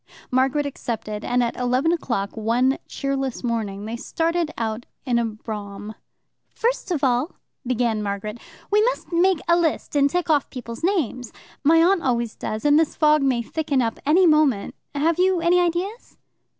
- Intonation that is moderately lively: No, wide, 6.1 semitones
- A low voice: No, very high, 270 Hz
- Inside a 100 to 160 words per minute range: No, average, 170 wpm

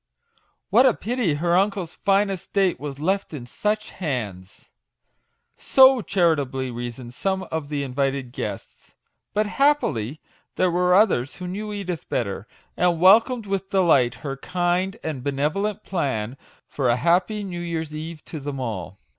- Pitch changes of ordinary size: No, wide, 6.3 semitones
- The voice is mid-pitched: Yes, medium, 170 Hz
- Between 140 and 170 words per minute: Yes, average, 150 wpm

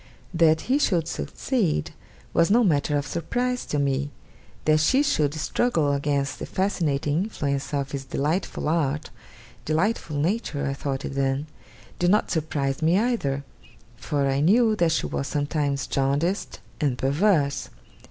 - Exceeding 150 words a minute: No, average, 145 wpm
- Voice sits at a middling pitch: Yes, medium, 150 Hz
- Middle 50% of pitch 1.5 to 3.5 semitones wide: No, average, 4.4 semitones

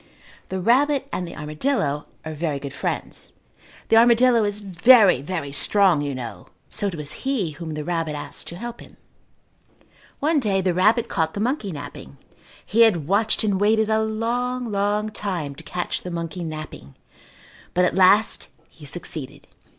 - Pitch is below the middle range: No, medium, 185 Hz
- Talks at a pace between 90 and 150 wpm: No, average, 165 wpm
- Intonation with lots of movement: Yes, wide, 6.1 semitones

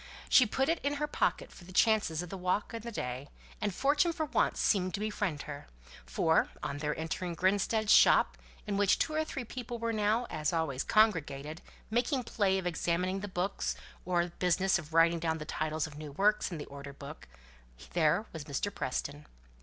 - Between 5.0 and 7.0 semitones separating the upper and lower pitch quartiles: Yes, wide, 5.6 semitones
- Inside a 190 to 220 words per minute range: Yes, average, 195 wpm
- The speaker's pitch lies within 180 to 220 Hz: Yes, medium, 185 Hz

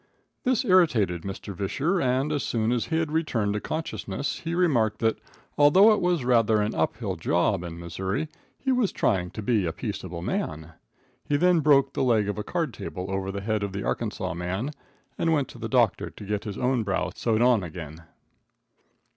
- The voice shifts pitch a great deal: Yes, wide, 7.3 semitones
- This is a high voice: No, low, 110 Hz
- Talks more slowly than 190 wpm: No, average, 195 wpm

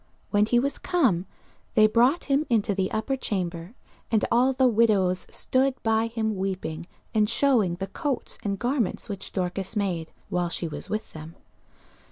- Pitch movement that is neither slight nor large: Yes, average, 4.6 semitones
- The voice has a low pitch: No, high, 215 Hz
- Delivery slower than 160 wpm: No, average, 165 wpm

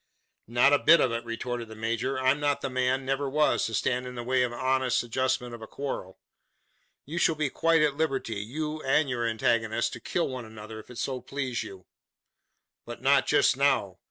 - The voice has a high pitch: No, low, 130 Hz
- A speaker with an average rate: No, fast, 210 wpm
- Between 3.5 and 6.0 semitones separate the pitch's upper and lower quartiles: No, average, 3.0 semitones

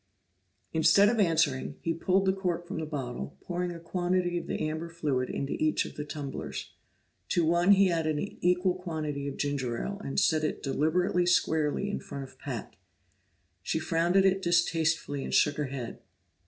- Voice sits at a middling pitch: Yes, medium, 165 Hz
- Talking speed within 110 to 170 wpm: No, average, 180 wpm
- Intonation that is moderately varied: Yes, average, 3.4 semitones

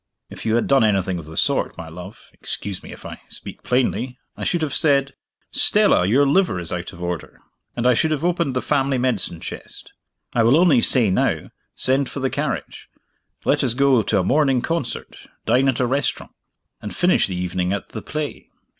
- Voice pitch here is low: Yes, low, 125 Hz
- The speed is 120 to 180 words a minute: No, average, 200 wpm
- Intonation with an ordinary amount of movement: No, wide, 6.1 semitones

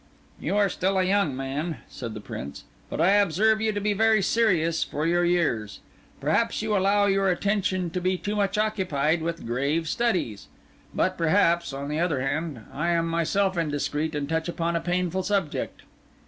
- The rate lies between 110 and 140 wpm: No, average, 180 wpm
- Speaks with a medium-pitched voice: Yes, medium, 175 Hz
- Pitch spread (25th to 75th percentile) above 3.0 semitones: Yes, average, 4.4 semitones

